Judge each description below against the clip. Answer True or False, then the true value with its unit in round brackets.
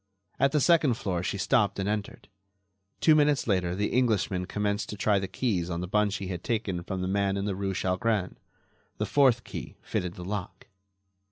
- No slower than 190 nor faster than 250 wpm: True (195 wpm)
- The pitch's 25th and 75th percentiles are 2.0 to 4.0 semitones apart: True (3.5 semitones)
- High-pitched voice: False (100 Hz)